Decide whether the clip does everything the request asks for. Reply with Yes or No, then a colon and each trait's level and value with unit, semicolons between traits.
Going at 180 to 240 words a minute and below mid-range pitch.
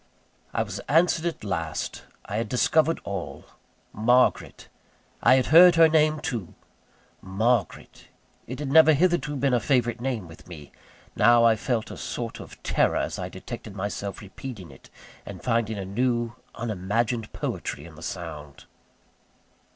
No: average, 150 wpm; low, 115 Hz